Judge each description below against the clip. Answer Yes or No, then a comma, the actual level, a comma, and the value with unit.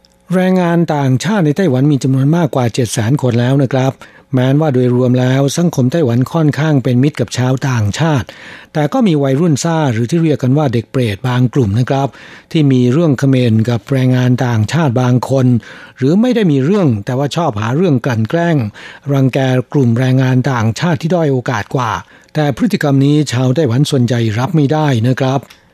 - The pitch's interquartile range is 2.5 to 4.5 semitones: Yes, average, 3.2 semitones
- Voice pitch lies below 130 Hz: No, low, 135 Hz